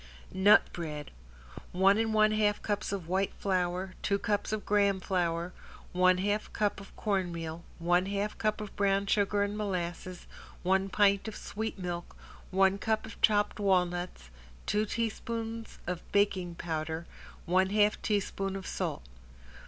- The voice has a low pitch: No, high, 195 Hz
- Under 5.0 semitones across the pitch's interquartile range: Yes, narrow, 2.6 semitones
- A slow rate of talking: No, average, 145 wpm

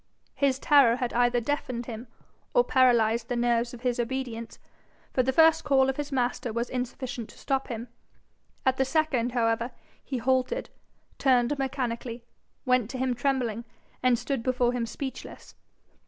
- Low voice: No, very high, 250 Hz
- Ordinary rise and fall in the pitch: No, narrow, 2.0 semitones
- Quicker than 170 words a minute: No, average, 155 wpm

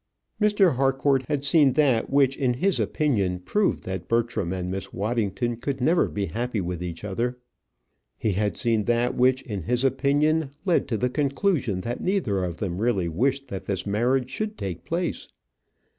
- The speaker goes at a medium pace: Yes, average, 175 wpm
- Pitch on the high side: No, low, 120 Hz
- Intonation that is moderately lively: No, wide, 5.7 semitones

